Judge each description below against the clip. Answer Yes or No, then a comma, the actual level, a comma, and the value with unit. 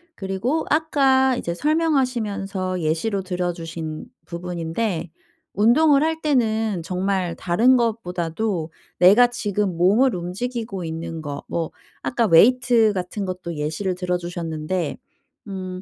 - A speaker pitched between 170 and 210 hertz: Yes, high, 190 Hz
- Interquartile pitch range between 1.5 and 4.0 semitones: No, wide, 5.5 semitones